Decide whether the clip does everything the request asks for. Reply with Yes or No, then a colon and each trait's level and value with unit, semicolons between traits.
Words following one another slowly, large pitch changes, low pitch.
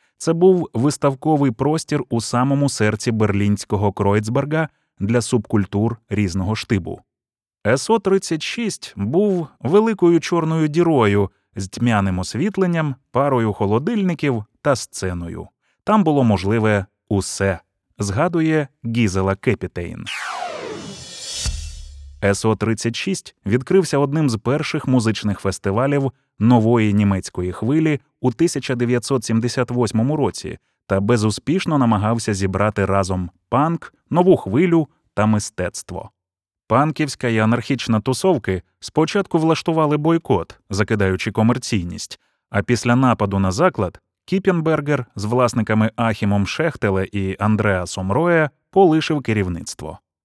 Yes: slow, 95 wpm; wide, 6.8 semitones; low, 120 Hz